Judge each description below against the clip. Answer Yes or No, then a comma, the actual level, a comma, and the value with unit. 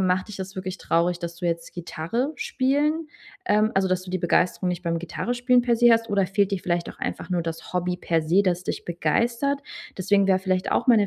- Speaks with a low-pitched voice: No, medium, 185 Hz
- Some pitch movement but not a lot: Yes, average, 4.7 semitones